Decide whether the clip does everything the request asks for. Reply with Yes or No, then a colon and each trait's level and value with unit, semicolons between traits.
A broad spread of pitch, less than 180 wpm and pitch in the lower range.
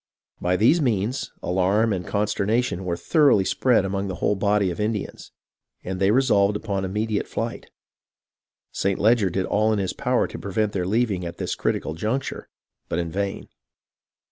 No: average, 2.7 semitones; average, 170 wpm; low, 100 Hz